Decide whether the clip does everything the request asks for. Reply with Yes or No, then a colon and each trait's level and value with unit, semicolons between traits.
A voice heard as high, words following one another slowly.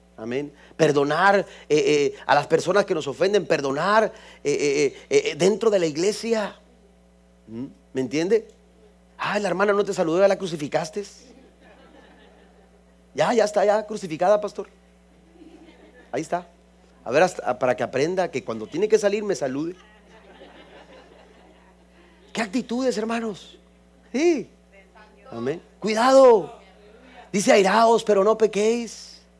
Yes: high, 200 Hz; slow, 120 wpm